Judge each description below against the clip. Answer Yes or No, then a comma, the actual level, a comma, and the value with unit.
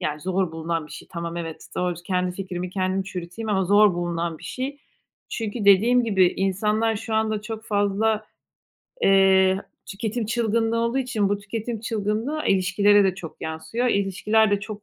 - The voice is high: Yes, high, 200 Hz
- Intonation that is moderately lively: Yes, average, 3.2 semitones